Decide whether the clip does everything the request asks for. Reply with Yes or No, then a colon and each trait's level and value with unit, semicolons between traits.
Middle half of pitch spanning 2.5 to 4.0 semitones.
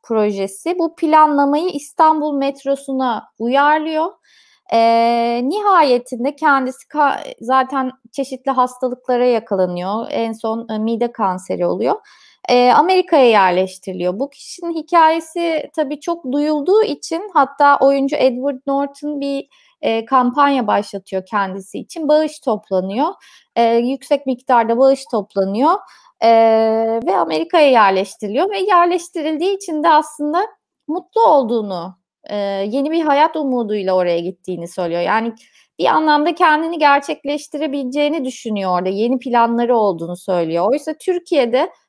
No: wide, 5.6 semitones